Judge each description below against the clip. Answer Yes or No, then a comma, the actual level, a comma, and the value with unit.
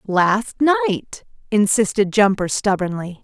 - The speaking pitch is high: Yes, high, 200 Hz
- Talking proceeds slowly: Yes, slow, 95 wpm